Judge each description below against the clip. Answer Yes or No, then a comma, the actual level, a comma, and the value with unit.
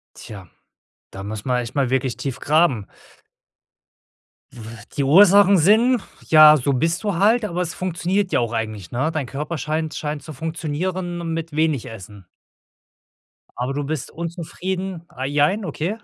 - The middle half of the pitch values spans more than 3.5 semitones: Yes, average, 5.1 semitones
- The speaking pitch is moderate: Yes, medium, 155 Hz